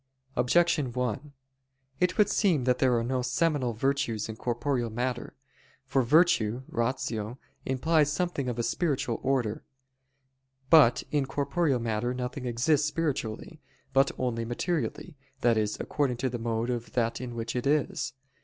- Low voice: Yes, low, 125 Hz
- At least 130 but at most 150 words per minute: Yes, average, 145 wpm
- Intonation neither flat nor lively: Yes, average, 3.6 semitones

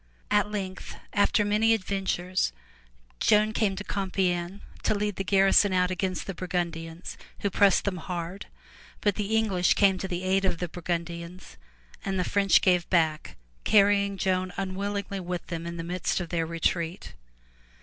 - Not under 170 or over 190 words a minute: No, average, 160 wpm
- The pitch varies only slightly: Yes, narrow, 2.3 semitones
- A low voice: No, medium, 185 Hz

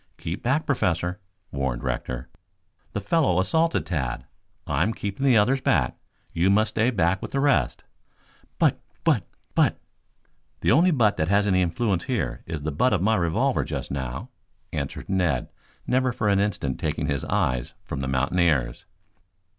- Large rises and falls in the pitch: Yes, wide, 7.7 semitones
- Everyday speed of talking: Yes, average, 165 wpm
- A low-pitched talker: Yes, very low, 95 Hz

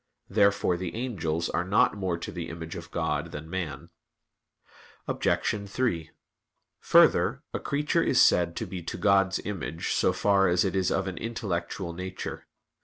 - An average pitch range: Yes, average, 3.1 semitones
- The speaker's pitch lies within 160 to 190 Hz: No, very low, 95 Hz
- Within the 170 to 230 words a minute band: No, average, 160 wpm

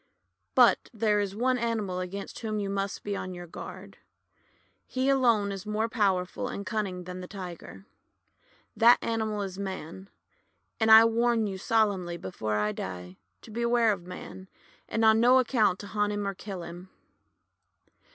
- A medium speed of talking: Yes, average, 165 wpm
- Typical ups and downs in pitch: Yes, average, 3.4 semitones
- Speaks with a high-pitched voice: Yes, high, 200 Hz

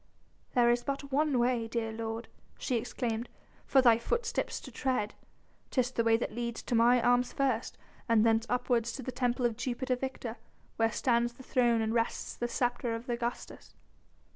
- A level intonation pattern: Yes, narrow, 1.7 semitones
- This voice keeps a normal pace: Yes, average, 175 wpm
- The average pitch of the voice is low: No, high, 240 Hz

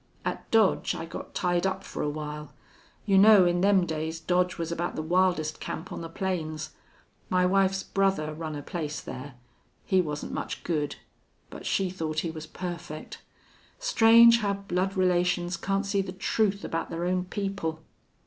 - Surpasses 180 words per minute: No, average, 170 wpm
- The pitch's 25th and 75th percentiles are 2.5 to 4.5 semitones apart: Yes, average, 3.3 semitones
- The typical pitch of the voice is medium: Yes, medium, 180 Hz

